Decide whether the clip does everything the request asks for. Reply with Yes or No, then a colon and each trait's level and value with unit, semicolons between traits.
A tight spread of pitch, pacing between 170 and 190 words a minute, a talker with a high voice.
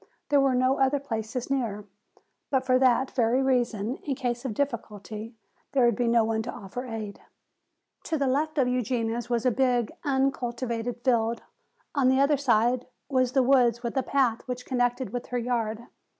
Yes: narrow, 2.3 semitones; average, 180 wpm; high, 245 Hz